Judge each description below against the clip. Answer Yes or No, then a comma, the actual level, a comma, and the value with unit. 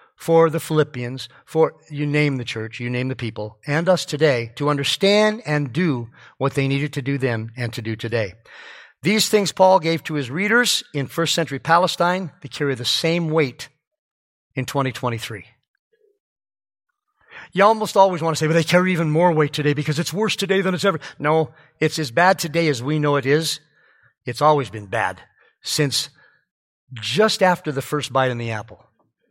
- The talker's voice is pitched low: No, medium, 150 Hz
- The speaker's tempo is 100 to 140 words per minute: No, average, 185 wpm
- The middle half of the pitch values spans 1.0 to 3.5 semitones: No, average, 4.9 semitones